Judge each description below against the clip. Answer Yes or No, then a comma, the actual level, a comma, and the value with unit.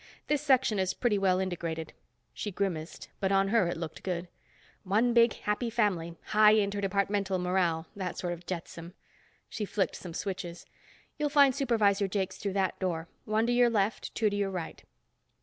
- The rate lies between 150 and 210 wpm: Yes, average, 170 wpm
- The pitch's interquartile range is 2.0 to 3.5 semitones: Yes, average, 3.1 semitones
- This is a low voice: No, high, 195 Hz